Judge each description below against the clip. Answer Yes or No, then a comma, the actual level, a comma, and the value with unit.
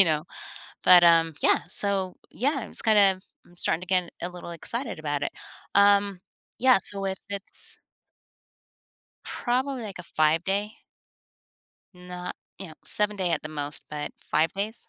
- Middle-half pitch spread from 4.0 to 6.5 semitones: No, average, 3.3 semitones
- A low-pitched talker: No, medium, 185 Hz